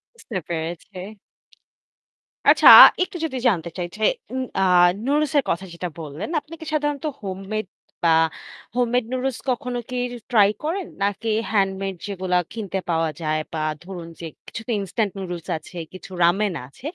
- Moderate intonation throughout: No, wide, 6.0 semitones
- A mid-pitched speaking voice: No, high, 195 Hz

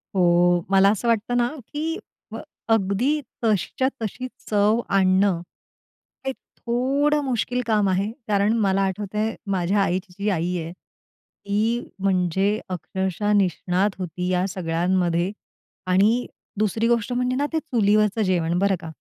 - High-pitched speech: Yes, high, 200 Hz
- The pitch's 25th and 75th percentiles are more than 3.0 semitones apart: Yes, average, 3.5 semitones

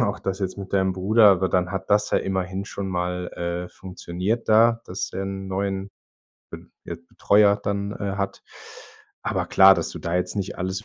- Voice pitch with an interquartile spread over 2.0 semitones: No, narrow, 1.6 semitones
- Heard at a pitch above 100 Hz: No, very low, 95 Hz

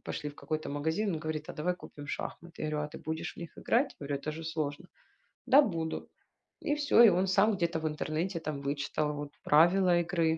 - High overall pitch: No, medium, 160 Hz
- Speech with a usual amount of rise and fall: Yes, average, 3.2 semitones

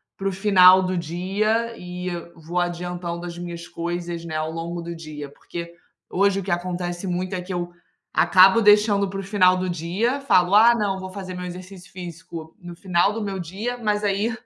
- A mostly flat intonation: Yes, narrow, 2.3 semitones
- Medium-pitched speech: Yes, medium, 180 Hz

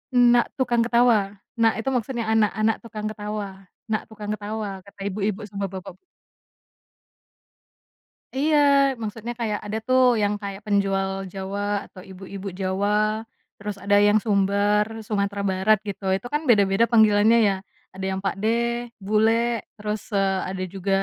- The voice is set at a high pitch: Yes, high, 205 Hz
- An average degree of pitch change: No, narrow, 2.1 semitones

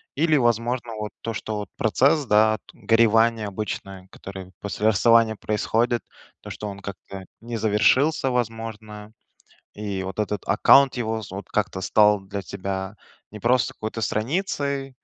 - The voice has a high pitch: No, low, 110 Hz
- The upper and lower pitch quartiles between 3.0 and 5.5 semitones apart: No, narrow, 2.4 semitones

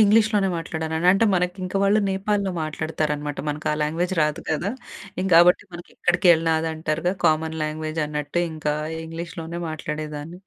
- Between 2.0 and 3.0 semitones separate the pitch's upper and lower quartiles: Yes, average, 2.7 semitones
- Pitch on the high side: No, medium, 165 Hz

